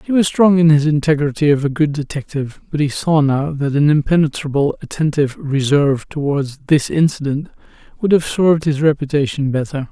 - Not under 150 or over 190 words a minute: Yes, average, 170 wpm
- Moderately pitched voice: Yes, medium, 150 Hz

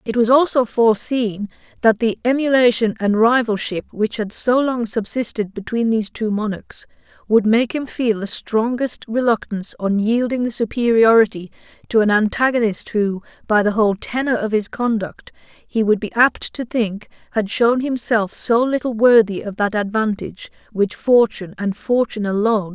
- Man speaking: No, female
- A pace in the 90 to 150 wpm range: No, average, 170 wpm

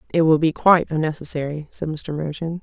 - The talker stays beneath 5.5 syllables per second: No, 5.8 syllables/s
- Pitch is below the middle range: No, medium, 155 Hz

